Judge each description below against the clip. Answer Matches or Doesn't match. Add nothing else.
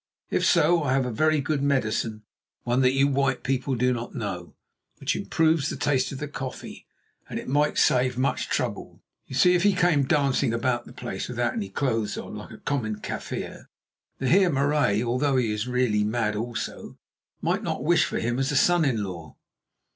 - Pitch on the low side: Matches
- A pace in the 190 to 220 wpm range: Matches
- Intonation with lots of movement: Doesn't match